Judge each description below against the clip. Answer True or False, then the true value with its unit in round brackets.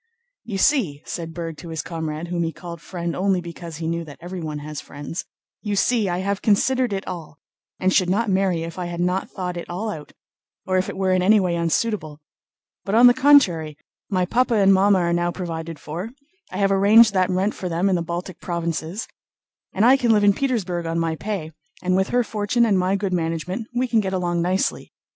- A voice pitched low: False (185 Hz)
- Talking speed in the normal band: False (210 wpm)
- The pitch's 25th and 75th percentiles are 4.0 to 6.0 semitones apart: False (3.4 semitones)